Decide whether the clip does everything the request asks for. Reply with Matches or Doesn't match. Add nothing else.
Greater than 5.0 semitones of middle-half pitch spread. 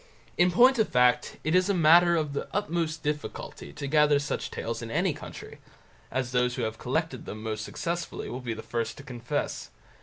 Matches